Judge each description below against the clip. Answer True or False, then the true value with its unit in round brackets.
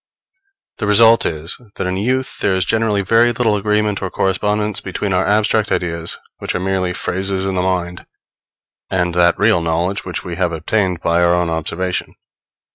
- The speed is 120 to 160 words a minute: False (175 wpm)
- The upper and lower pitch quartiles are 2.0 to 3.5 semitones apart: True (3.0 semitones)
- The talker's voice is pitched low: True (95 Hz)